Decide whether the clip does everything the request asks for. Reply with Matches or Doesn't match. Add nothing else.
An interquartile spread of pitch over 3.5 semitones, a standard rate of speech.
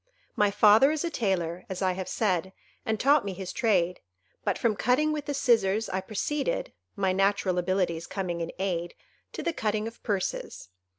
Matches